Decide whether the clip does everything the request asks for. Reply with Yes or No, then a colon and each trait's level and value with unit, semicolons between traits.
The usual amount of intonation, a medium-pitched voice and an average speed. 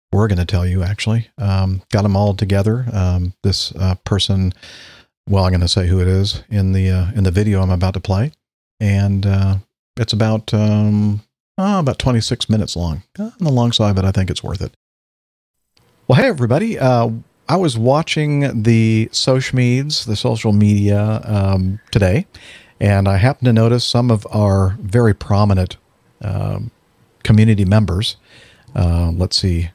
No: average, 3.4 semitones; low, 105 Hz; average, 170 wpm